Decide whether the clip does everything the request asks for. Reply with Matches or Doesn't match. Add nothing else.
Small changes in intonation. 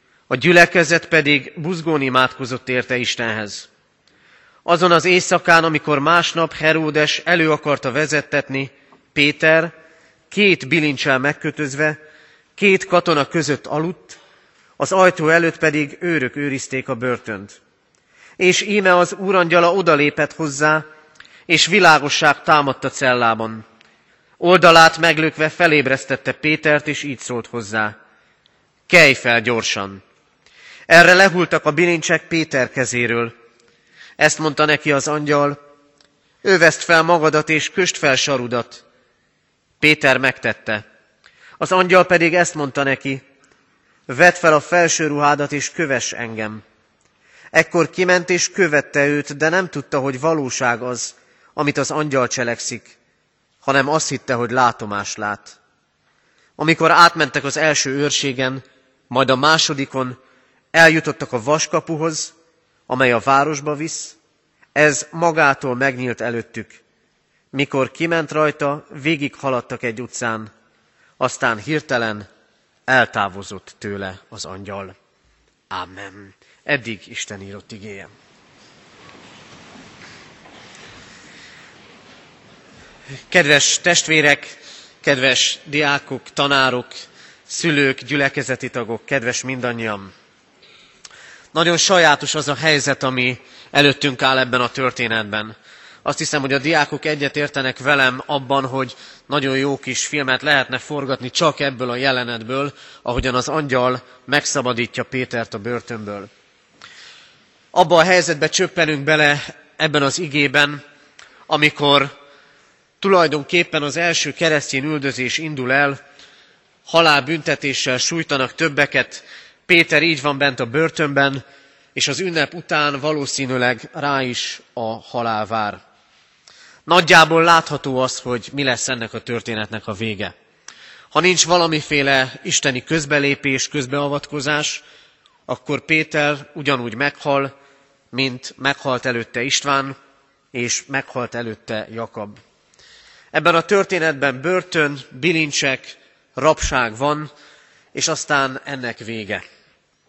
Doesn't match